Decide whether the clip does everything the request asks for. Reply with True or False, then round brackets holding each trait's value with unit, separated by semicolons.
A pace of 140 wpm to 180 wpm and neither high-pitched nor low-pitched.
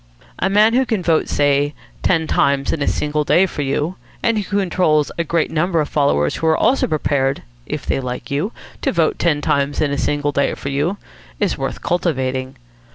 False (200 wpm; 150 Hz)